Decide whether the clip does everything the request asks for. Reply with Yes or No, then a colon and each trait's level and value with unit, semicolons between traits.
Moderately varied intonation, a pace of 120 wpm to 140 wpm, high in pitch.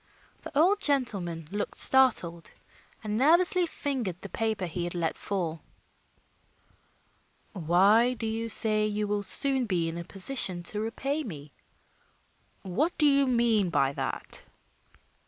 No: wide, 7.1 semitones; slow, 135 wpm; high, 215 Hz